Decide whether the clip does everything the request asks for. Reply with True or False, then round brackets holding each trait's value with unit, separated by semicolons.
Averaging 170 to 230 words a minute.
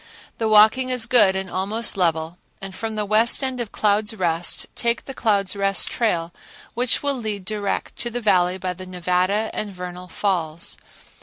True (175 wpm)